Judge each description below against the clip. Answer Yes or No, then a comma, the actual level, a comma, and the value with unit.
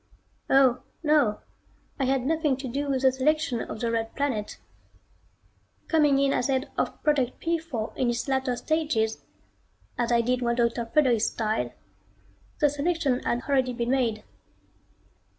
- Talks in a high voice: Yes, very high, 260 Hz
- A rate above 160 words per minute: No, average, 150 wpm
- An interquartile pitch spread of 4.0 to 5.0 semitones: No, average, 3.3 semitones